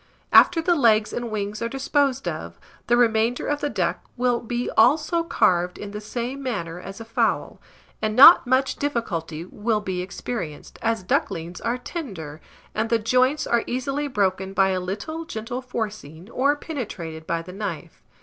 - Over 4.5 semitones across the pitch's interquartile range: Yes, average, 5.2 semitones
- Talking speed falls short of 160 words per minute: No, average, 170 wpm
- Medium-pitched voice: No, high, 225 Hz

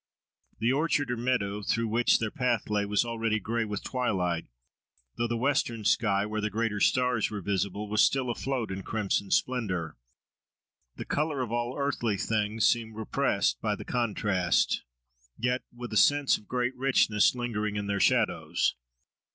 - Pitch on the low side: Yes, low, 115 Hz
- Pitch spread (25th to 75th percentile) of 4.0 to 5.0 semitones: No, average, 3.1 semitones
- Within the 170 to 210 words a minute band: No, average, 160 wpm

